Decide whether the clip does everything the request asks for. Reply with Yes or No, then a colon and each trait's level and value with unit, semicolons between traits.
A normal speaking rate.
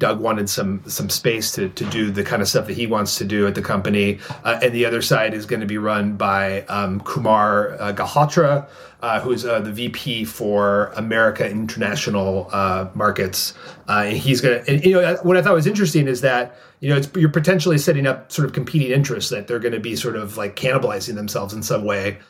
No: fast, 220 wpm